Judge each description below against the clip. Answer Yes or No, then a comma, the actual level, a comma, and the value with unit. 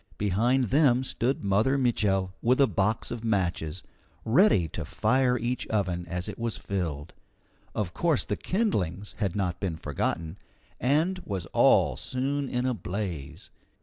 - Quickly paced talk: No, average, 150 wpm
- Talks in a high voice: No, low, 105 Hz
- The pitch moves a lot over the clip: Yes, wide, 5.9 semitones